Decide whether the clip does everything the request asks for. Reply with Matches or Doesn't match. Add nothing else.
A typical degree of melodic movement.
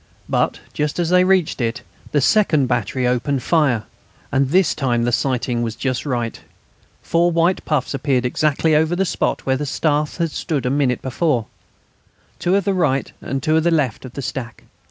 Matches